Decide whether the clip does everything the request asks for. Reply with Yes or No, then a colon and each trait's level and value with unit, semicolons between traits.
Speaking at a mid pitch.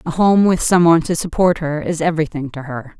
Yes: medium, 160 Hz